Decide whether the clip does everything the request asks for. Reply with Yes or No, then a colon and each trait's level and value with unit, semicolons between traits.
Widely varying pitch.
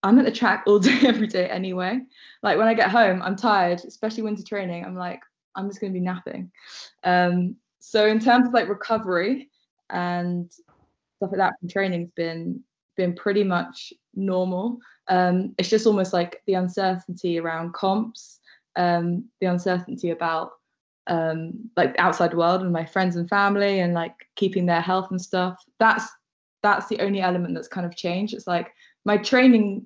No: average, 3.6 semitones